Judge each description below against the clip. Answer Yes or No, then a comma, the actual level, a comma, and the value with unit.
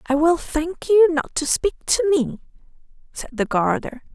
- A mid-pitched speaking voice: No, very high, 310 Hz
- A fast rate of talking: No, average, 175 wpm